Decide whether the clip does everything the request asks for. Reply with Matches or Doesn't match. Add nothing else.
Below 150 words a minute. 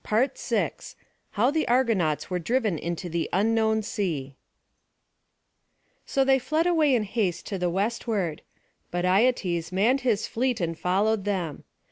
Matches